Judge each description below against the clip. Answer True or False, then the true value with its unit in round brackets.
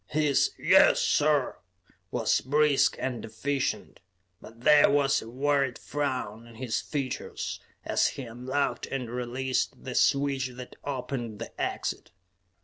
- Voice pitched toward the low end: True (130 Hz)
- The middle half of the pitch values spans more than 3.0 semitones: False (2.7 semitones)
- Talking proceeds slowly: True (130 wpm)